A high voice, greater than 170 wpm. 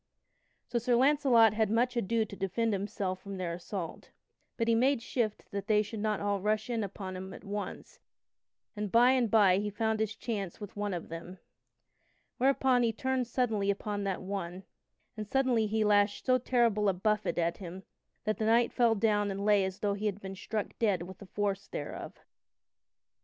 Yes: high, 210 Hz; average, 190 wpm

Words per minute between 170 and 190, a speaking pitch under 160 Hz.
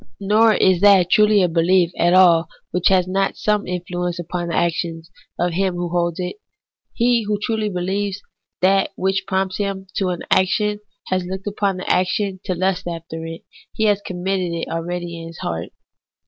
No: average, 180 wpm; medium, 185 Hz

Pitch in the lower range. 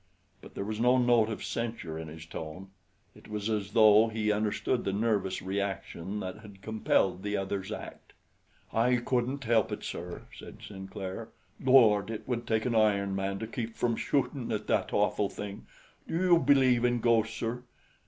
Yes: low, 110 Hz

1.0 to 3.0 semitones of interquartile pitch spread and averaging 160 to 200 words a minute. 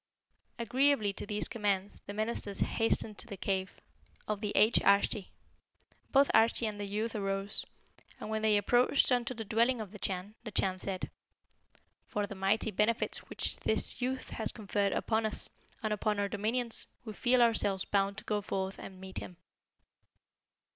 Yes: narrow, 2.4 semitones; average, 170 wpm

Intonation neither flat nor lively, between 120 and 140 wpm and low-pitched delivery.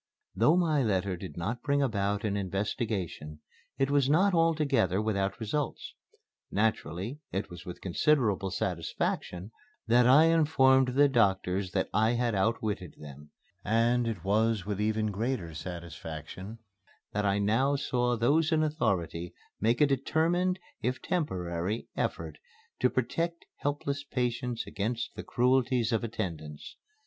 No: wide, 5.8 semitones; slow, 135 wpm; low, 115 Hz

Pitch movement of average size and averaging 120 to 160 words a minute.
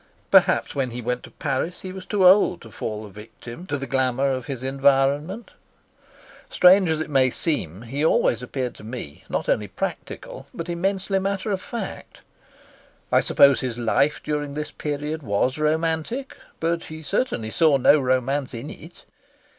No: average, 4.9 semitones; average, 170 wpm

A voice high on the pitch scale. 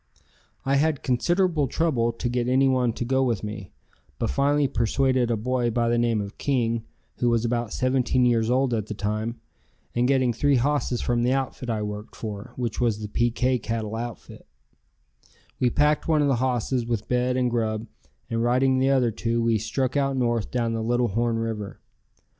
No: low, 120 Hz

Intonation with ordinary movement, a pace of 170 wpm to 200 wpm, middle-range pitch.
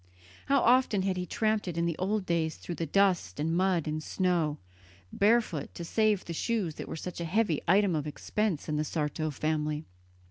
Yes: average, 4.5 semitones; average, 190 wpm; medium, 175 Hz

